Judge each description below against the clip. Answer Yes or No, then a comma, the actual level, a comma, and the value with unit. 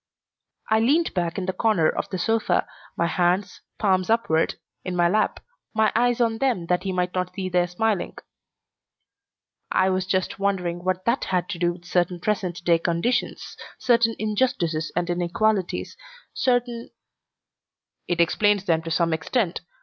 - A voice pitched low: No, medium, 185 Hz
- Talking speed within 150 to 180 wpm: Yes, average, 160 wpm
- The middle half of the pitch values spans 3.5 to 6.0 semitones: Yes, average, 3.8 semitones